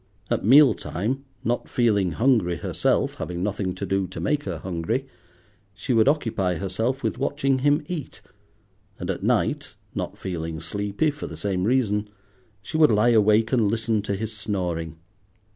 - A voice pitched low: Yes, low, 105 Hz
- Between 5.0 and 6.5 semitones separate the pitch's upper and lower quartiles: Yes, average, 5.3 semitones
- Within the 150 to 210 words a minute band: Yes, average, 160 wpm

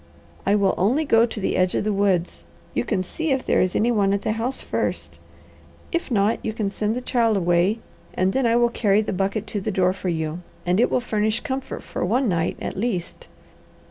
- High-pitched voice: Yes, high, 210 Hz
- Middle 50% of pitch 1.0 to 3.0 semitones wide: No, average, 3.9 semitones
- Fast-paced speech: Yes, fast, 225 wpm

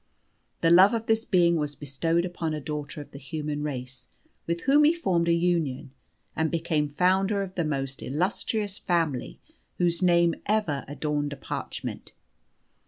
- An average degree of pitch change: Yes, average, 3.8 semitones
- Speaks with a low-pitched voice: No, medium, 165 Hz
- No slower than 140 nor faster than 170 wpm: Yes, average, 160 wpm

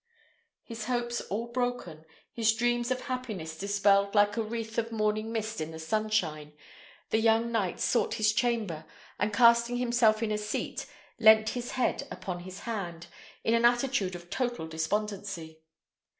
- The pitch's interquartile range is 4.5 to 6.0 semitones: No, average, 3.2 semitones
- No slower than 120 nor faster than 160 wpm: Yes, average, 155 wpm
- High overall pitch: Yes, high, 220 Hz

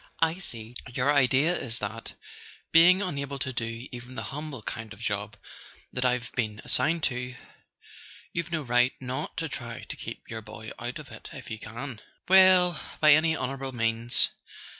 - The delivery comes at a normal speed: Yes, average, 165 wpm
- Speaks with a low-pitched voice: Yes, low, 125 Hz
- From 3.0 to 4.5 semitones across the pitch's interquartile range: No, average, 4.9 semitones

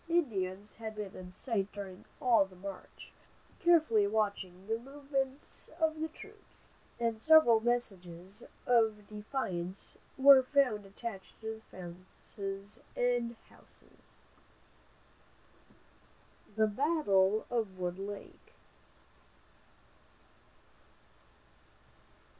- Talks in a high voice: Yes, high, 220 Hz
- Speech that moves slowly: Yes, slow, 90 wpm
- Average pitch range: Yes, average, 4.6 semitones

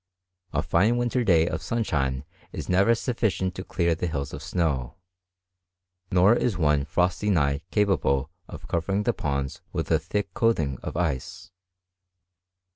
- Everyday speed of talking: Yes, average, 155 wpm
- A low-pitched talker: Yes, very low, 85 Hz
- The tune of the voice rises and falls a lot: Yes, wide, 5.8 semitones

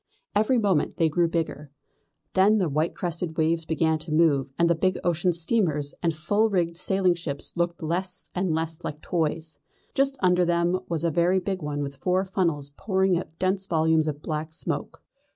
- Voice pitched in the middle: Yes, medium, 170 Hz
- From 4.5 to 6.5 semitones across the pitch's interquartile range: No, average, 2.8 semitones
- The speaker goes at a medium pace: Yes, average, 190 wpm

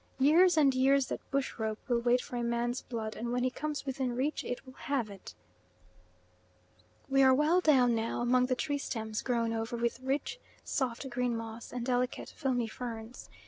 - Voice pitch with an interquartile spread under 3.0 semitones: Yes, narrow, 2.4 semitones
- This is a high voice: Yes, very high, 250 Hz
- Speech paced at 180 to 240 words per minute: Yes, average, 185 wpm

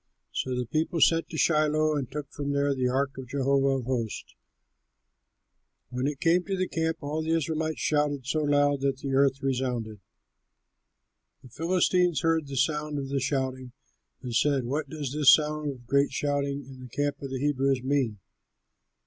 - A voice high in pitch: No, medium, 140 Hz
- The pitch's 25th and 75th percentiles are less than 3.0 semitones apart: Yes, narrow, 2.4 semitones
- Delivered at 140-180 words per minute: Yes, average, 175 wpm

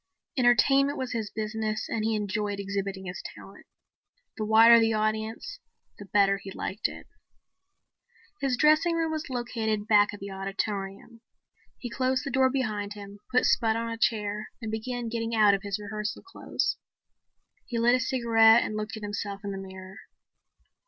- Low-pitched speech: No, high, 220 Hz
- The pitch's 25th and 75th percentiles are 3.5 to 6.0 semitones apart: No, average, 2.8 semitones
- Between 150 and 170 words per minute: Yes, average, 165 wpm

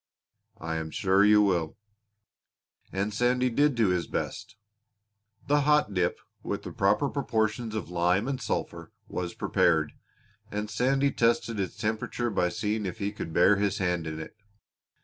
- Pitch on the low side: Yes, low, 105 Hz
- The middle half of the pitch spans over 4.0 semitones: Yes, average, 4.7 semitones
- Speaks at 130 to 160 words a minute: Yes, average, 155 wpm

